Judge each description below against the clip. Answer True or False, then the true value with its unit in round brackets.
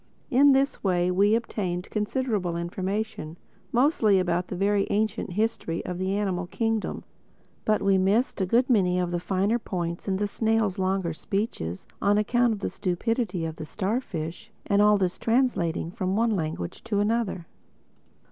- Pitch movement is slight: False (3.7 semitones)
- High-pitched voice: True (195 Hz)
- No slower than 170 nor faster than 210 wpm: False (160 wpm)